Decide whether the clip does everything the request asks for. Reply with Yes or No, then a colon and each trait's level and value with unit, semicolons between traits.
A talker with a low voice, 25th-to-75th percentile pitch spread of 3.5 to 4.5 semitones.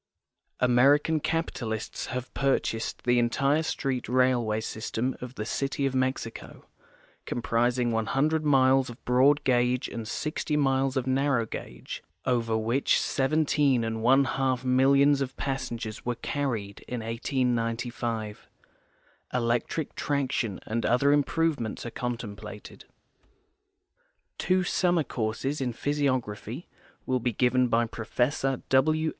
No: low, 125 Hz; average, 2.9 semitones